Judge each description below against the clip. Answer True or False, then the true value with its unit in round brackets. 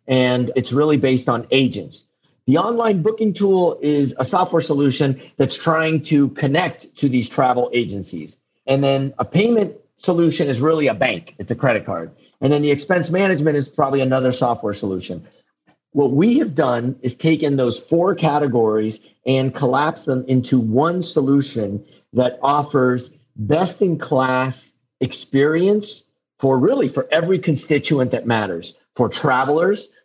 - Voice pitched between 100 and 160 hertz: True (140 Hz)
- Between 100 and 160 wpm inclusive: True (145 wpm)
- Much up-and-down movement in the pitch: False (3.9 semitones)